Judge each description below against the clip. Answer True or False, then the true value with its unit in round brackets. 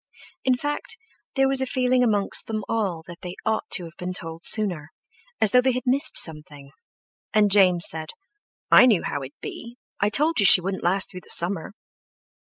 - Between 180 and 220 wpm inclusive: True (190 wpm)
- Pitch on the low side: False (200 Hz)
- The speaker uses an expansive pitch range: True (6.4 semitones)